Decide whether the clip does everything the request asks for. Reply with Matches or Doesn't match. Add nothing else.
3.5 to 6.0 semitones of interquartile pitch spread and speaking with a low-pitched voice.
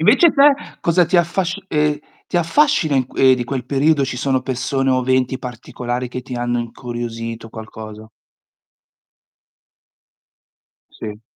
Matches